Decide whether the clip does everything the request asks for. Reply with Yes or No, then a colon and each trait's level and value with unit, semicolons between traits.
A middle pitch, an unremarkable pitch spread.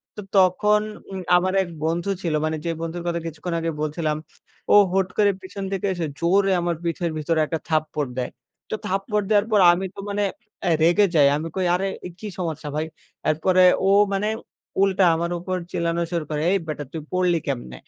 Yes: medium, 175 Hz; average, 3.3 semitones